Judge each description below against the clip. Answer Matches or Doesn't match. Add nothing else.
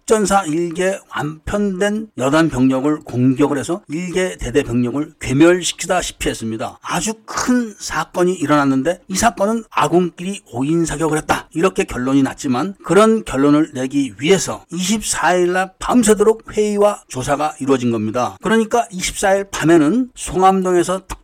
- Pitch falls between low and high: Matches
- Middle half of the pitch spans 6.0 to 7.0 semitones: Doesn't match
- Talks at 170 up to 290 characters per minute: Doesn't match